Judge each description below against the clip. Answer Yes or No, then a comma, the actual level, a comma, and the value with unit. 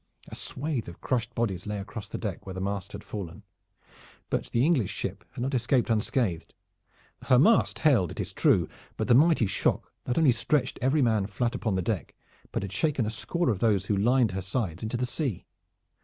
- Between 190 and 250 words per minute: Yes, fast, 205 wpm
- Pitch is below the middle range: Yes, low, 115 Hz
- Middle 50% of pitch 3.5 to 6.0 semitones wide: Yes, average, 4.6 semitones